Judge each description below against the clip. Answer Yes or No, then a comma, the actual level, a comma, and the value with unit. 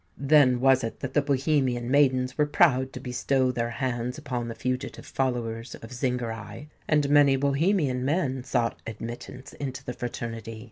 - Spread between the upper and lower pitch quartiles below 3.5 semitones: Yes, narrow, 2.5 semitones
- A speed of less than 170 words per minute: Yes, average, 155 wpm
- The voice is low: Yes, low, 130 Hz